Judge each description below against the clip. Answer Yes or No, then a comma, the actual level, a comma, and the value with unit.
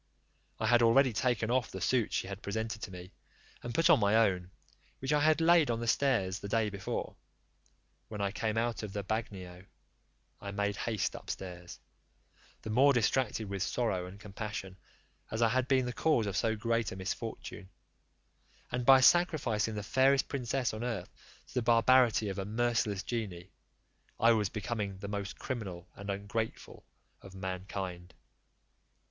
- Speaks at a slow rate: No, average, 165 wpm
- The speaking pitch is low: Yes, low, 110 Hz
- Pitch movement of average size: Yes, average, 3.6 semitones